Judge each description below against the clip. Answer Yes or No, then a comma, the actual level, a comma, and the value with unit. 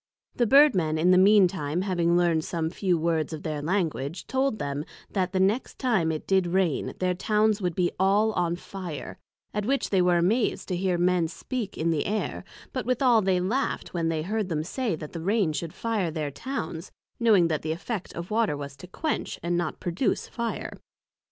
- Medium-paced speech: Yes, average, 195 wpm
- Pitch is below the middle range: No, medium, 180 Hz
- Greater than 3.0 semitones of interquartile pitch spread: Yes, average, 4.4 semitones